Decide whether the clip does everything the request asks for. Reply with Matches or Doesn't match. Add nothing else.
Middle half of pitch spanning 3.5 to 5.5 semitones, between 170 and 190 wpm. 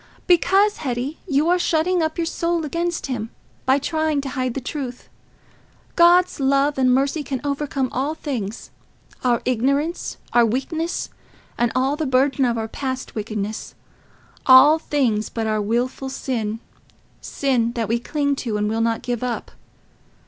Doesn't match